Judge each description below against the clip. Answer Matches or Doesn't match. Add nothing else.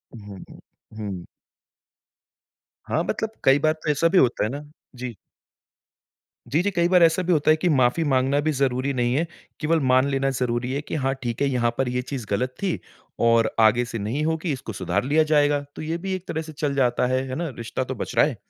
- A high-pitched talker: Doesn't match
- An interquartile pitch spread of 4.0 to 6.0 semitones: Matches